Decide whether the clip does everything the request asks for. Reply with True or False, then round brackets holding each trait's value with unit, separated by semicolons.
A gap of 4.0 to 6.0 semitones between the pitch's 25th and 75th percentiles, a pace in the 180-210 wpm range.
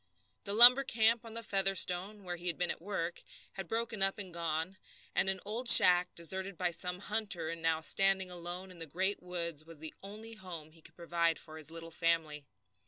False (3.0 semitones; 205 wpm)